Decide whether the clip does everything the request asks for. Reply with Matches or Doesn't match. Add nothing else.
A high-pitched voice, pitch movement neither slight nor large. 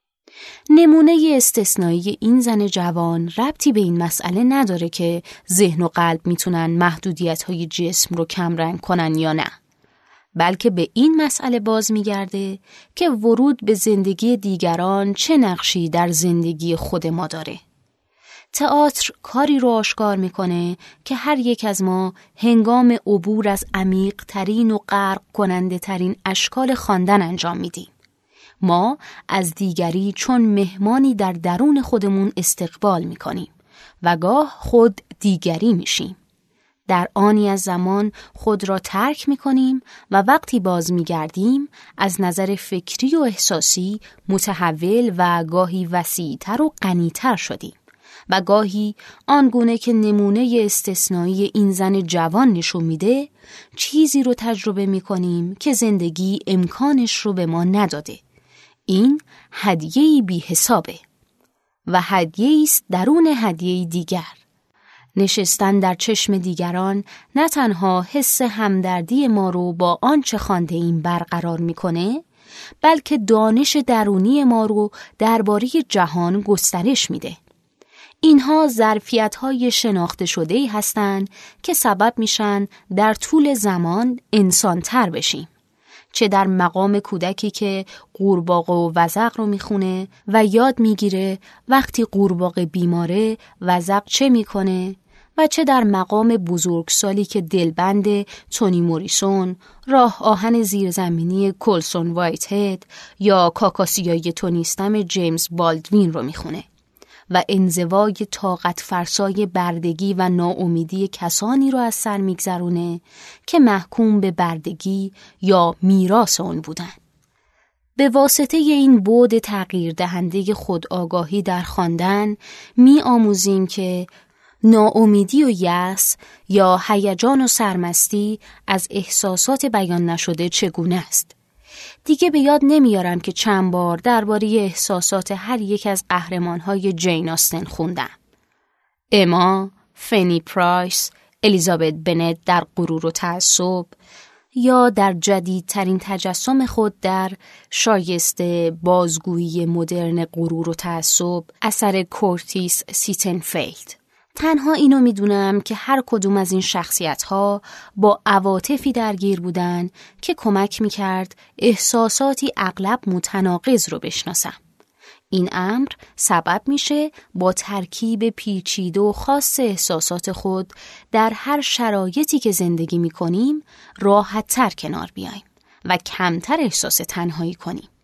Matches